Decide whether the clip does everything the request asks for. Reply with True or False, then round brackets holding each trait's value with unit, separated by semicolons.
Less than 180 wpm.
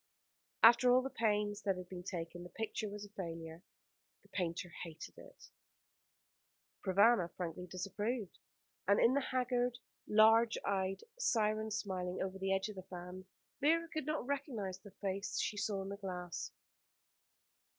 True (150 wpm)